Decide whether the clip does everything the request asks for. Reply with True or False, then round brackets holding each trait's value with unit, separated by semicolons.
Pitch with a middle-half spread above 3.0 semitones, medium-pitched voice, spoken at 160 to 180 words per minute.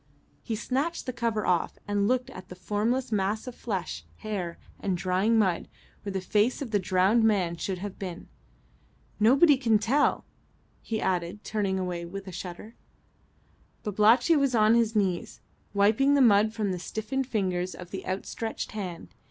False (3.8 semitones; 210 Hz; 165 wpm)